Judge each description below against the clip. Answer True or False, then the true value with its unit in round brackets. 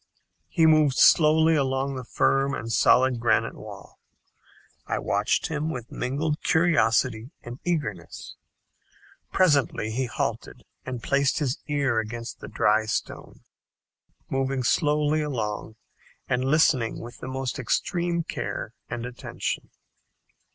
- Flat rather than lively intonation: False (4.3 semitones)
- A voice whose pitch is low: True (130 Hz)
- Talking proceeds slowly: True (120 wpm)